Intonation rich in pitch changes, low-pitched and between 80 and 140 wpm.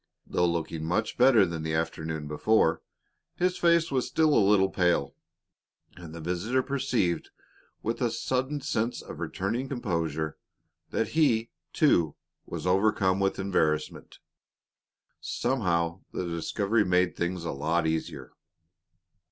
Yes: wide, 6.2 semitones; very low, 95 Hz; slow, 135 wpm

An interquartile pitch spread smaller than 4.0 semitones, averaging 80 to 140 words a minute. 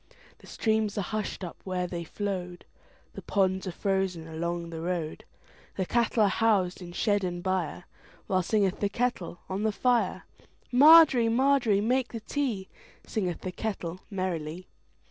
Yes: average, 3.6 semitones; slow, 135 wpm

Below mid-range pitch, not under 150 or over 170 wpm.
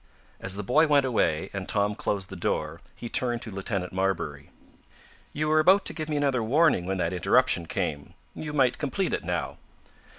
No: low, 110 Hz; average, 190 wpm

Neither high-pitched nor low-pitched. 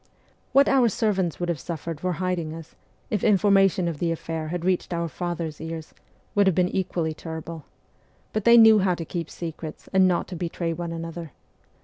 Yes: medium, 175 Hz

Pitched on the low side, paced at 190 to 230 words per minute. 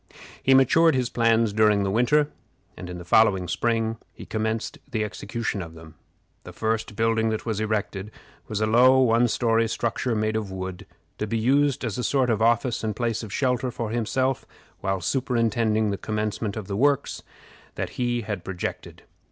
No: low, 110 Hz; average, 180 wpm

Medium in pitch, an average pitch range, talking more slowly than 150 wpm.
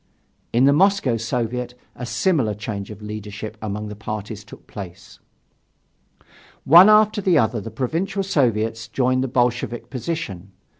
No: low, 120 Hz; average, 4.8 semitones; average, 140 wpm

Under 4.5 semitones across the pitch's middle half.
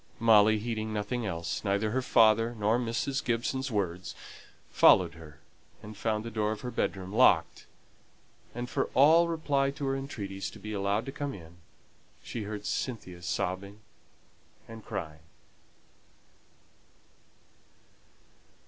Yes: average, 3.6 semitones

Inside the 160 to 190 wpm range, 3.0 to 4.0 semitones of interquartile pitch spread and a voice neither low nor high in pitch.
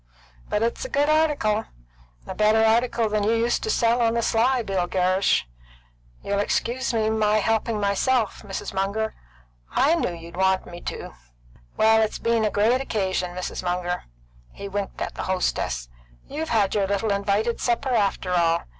No: average, 165 wpm; average, 3.3 semitones; high, 215 Hz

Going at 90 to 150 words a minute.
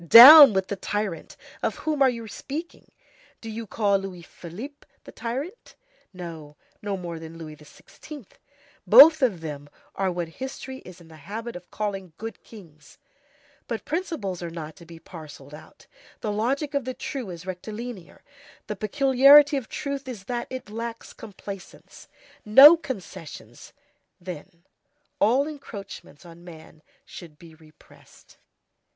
Yes: average, 145 wpm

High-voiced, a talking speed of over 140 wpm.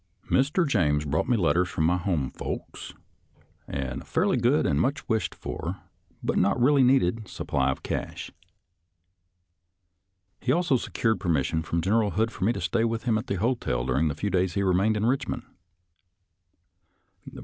No: low, 100 Hz; average, 170 wpm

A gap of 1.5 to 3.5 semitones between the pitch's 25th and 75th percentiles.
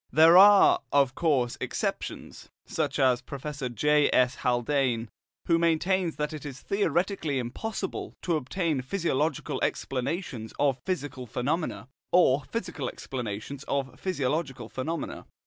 No: average, 4.7 semitones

